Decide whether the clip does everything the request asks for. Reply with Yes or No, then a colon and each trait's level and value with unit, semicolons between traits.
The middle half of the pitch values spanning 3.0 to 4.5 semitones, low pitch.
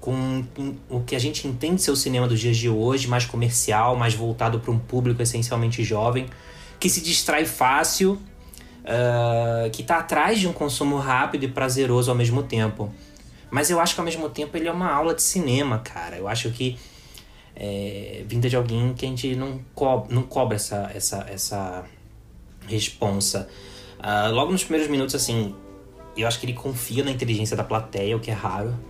Yes: average, 3.6 semitones; low, 120 Hz